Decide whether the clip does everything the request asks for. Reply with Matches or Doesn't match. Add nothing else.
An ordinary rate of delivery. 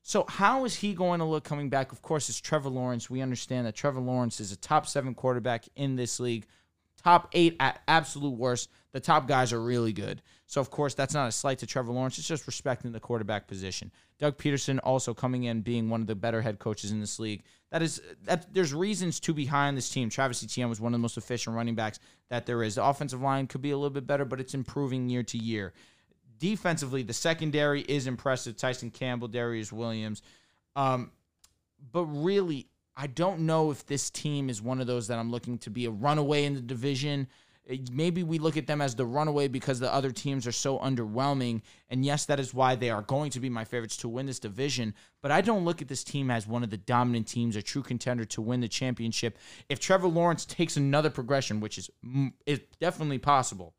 Doesn't match